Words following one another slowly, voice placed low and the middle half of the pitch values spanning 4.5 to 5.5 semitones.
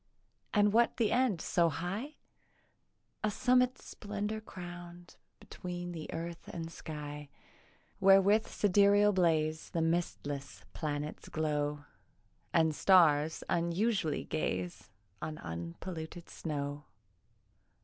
No: slow, 100 wpm; medium, 170 Hz; average, 4.9 semitones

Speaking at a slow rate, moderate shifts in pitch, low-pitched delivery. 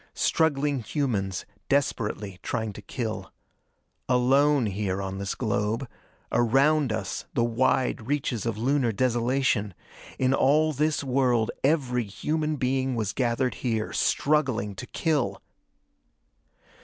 Yes: slow, 115 wpm; average, 4.2 semitones; low, 125 Hz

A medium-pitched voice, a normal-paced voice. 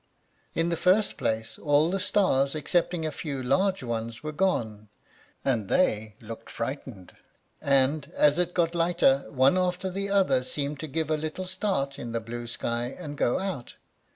Yes: medium, 145 Hz; average, 170 wpm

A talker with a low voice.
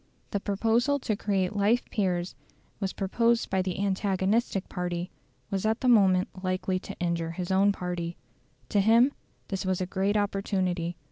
No: high, 195 Hz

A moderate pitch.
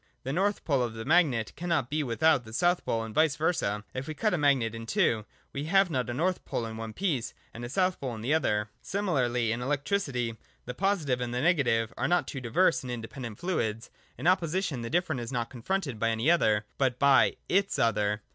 No: low, 130 Hz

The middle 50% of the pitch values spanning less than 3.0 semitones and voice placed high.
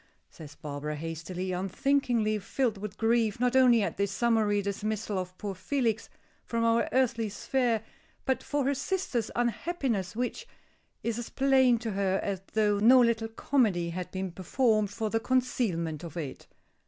No: average, 4.4 semitones; high, 220 Hz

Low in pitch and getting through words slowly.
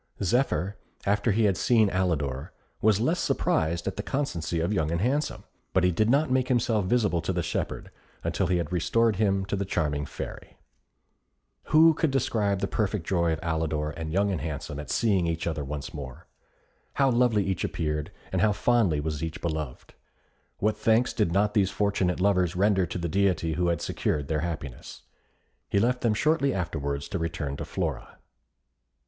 No: very low, 95 Hz; average, 180 wpm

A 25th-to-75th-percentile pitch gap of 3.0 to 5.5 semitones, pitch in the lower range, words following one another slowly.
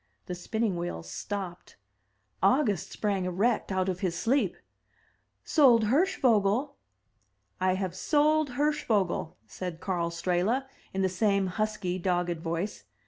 No: average, 4.5 semitones; high, 195 Hz; slow, 120 wpm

